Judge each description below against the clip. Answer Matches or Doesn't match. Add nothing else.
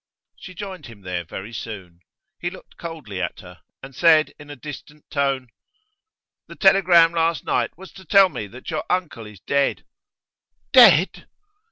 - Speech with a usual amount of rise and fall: Doesn't match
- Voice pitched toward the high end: Doesn't match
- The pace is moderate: Matches